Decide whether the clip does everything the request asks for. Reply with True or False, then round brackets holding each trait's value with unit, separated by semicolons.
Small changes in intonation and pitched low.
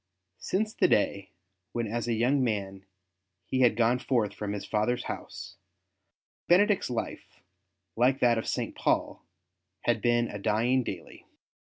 False (3.1 semitones; 120 Hz)